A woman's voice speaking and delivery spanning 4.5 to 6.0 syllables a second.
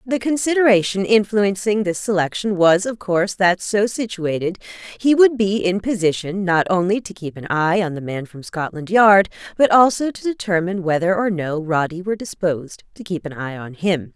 Yes: female; 5.1 syllables/s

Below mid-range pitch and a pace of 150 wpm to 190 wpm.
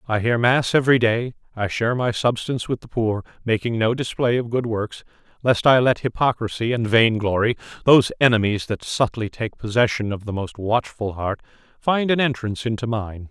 Yes: low, 115 Hz; average, 180 wpm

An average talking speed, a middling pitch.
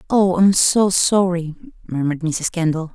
Yes: average, 145 wpm; medium, 180 Hz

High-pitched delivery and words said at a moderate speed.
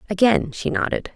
Yes: high, 210 Hz; average, 155 wpm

